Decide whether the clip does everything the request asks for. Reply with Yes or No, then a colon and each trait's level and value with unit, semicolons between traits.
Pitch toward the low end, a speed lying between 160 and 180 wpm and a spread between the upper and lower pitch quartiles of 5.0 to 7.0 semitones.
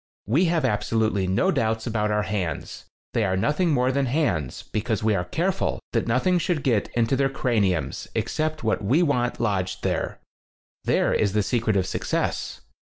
Yes: low, 115 Hz; average, 175 wpm; average, 5.3 semitones